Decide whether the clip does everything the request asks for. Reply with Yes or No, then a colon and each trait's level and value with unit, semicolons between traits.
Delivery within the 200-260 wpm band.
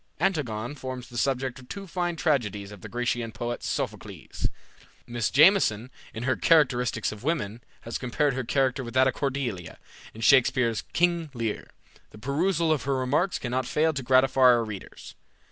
No: average, 165 wpm